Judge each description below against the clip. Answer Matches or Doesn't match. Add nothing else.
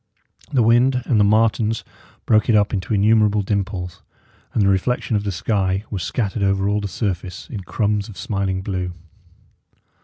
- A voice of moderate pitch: Doesn't match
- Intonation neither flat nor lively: Doesn't match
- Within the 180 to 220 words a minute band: Doesn't match